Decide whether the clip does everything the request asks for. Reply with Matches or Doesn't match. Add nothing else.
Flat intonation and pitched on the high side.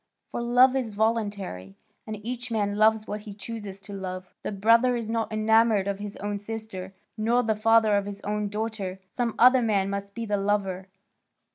Matches